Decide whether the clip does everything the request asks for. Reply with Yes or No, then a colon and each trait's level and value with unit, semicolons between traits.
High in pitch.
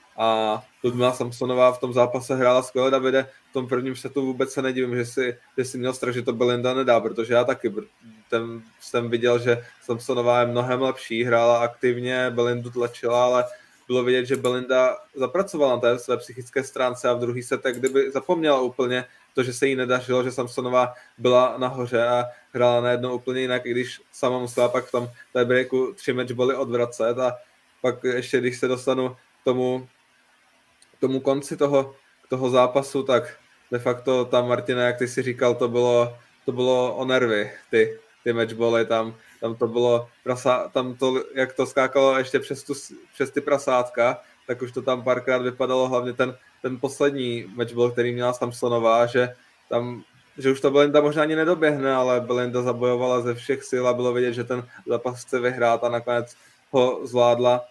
No: low, 125 Hz